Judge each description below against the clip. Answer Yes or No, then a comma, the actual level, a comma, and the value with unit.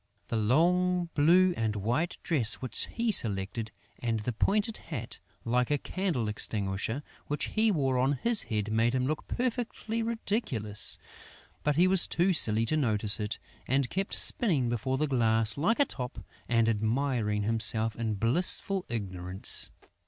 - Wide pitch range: Yes, wide, 8.0 semitones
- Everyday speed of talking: Yes, average, 150 wpm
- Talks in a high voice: No, low, 125 Hz